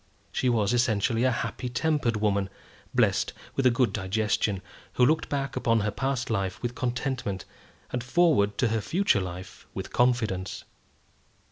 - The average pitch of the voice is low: Yes, low, 120 Hz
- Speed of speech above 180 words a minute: No, average, 150 wpm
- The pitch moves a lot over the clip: No, average, 4.0 semitones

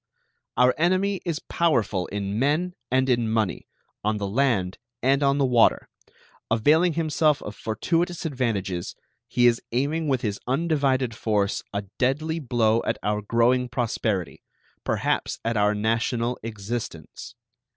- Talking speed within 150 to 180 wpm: No, slow, 135 wpm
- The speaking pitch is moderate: No, low, 120 Hz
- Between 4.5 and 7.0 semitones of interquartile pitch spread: Yes, average, 5.1 semitones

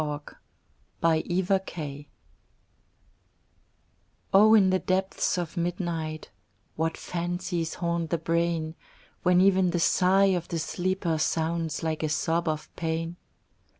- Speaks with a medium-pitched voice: Yes, medium, 170 Hz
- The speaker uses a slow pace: Yes, slow, 115 wpm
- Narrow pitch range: Yes, narrow, 2.2 semitones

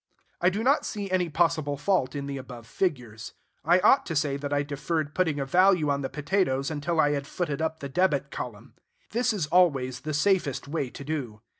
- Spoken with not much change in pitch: No, average, 4.3 semitones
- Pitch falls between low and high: Yes, medium, 145 Hz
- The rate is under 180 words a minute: No, fast, 205 wpm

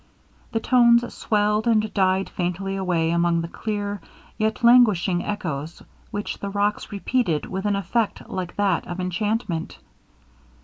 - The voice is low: No, high, 200 Hz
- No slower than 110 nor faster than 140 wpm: Yes, slow, 135 wpm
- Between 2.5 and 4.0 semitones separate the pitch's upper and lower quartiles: Yes, average, 3.5 semitones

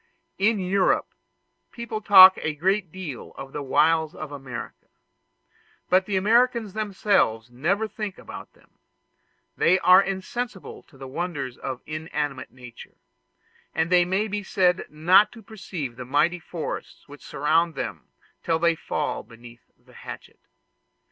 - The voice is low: No, medium, 175 Hz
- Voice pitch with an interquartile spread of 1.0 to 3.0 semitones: No, average, 5.2 semitones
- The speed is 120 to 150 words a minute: Yes, average, 140 wpm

